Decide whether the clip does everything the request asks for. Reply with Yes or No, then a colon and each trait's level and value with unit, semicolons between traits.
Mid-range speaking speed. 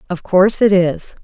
Yes: average, 195 wpm